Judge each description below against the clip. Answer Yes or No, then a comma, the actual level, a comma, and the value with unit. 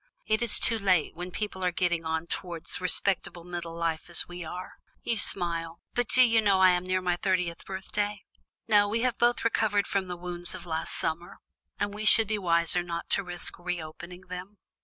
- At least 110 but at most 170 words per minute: No, average, 200 wpm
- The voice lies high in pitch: No, medium, 180 Hz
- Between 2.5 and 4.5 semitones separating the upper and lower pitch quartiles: Yes, average, 2.9 semitones